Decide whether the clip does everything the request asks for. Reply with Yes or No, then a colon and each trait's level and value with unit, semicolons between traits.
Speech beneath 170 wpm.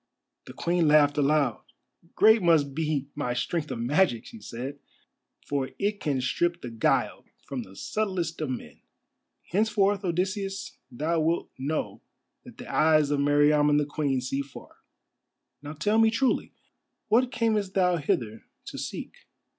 Yes: average, 145 wpm